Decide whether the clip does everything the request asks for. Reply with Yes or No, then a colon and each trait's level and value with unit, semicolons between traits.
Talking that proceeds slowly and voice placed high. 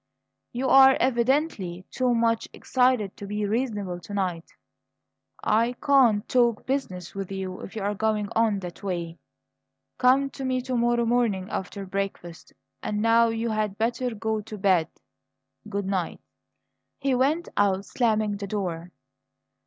No: average, 145 wpm; high, 215 Hz